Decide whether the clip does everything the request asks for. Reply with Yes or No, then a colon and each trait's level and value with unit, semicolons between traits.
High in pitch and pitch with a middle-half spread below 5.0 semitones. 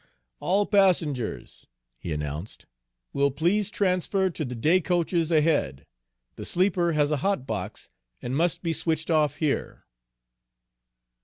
No: medium, 160 Hz; average, 4.5 semitones